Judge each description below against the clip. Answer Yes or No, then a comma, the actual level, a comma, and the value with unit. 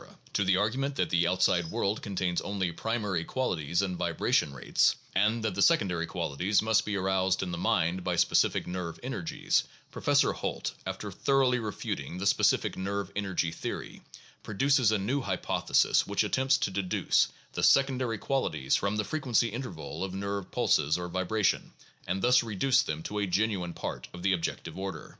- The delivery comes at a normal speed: Yes, average, 170 wpm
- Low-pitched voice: Yes, low, 100 Hz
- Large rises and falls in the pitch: No, average, 3.8 semitones